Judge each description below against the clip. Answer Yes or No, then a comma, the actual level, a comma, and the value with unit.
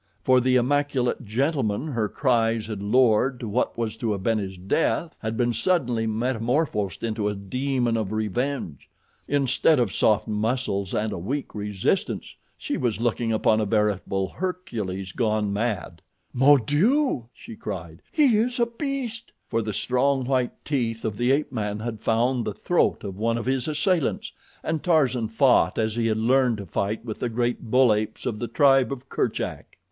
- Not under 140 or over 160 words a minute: No, average, 175 wpm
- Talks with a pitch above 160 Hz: No, low, 115 Hz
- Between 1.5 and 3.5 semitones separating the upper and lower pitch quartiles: No, average, 3.9 semitones